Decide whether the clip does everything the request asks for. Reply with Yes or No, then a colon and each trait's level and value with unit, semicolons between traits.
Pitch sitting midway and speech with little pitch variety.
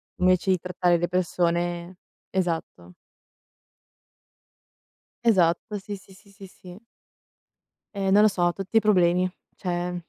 Yes: medium, 180 Hz; narrow, 1.9 semitones